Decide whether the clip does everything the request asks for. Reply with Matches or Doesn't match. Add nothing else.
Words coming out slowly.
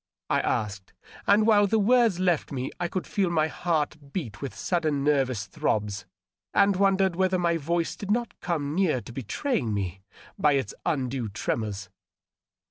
Doesn't match